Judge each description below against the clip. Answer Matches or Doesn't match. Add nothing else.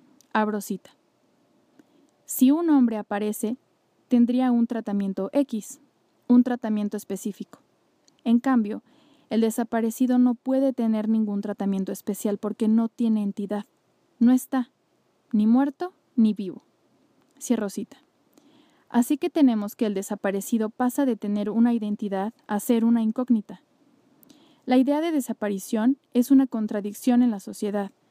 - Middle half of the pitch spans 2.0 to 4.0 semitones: Doesn't match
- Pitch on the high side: Matches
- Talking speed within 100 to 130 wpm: Matches